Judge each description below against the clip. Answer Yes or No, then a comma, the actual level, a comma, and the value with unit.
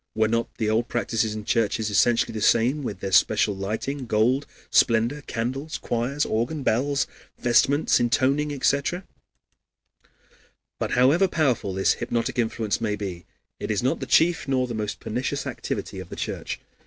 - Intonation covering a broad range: No, average, 3.9 semitones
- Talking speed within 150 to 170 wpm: Yes, average, 155 wpm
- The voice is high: No, low, 120 Hz